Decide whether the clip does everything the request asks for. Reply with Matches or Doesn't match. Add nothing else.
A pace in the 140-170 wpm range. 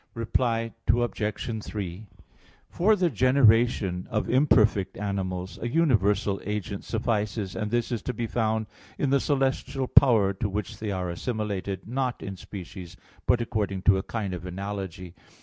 Matches